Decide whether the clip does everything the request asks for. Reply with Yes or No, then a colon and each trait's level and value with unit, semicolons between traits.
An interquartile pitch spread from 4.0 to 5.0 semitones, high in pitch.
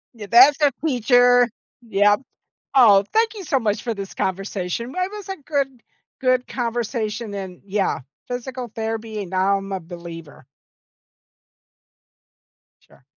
Yes: average, 4.5 semitones; high, 225 Hz